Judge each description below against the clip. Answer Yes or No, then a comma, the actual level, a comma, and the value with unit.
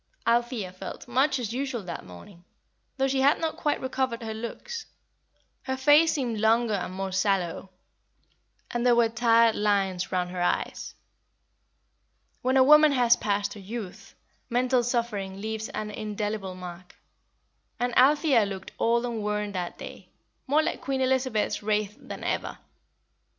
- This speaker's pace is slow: No, average, 150 wpm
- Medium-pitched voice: No, high, 230 Hz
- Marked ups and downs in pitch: No, average, 4.5 semitones